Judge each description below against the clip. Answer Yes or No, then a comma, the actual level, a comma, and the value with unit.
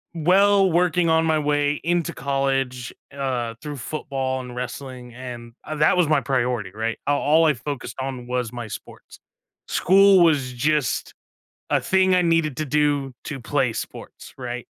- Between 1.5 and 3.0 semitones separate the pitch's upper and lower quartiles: No, average, 4.1 semitones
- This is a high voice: No, medium, 140 Hz